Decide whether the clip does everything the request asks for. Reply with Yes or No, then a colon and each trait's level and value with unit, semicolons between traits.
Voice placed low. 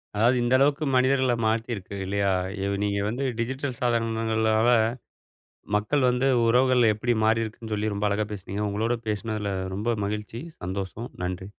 Yes: low, 110 Hz